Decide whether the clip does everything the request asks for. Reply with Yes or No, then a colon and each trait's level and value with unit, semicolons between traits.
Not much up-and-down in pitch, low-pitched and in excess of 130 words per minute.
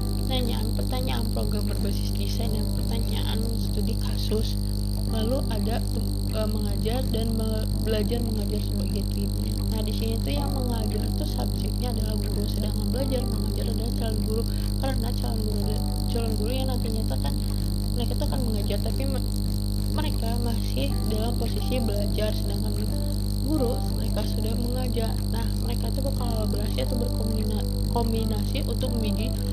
Yes: narrow, 0.6 semitones; low, 100 Hz; fast, 140 wpm